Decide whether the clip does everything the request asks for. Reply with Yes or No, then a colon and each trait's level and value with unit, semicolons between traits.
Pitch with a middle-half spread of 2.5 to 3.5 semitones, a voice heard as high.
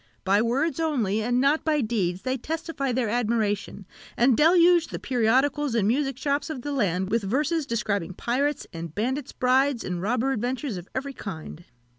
No: average, 5.2 semitones; very high, 250 Hz